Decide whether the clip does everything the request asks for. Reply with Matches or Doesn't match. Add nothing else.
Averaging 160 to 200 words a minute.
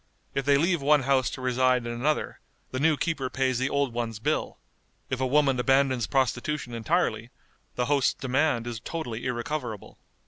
Matches